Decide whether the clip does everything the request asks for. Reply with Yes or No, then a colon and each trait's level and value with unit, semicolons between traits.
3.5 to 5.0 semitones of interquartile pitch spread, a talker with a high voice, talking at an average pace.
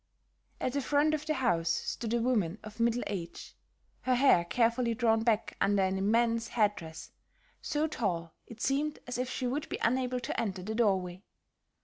Yes: average, 4.4 semitones; high, 230 Hz; average, 180 wpm